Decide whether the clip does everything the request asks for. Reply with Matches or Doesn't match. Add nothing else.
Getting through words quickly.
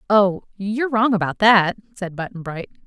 Doesn't match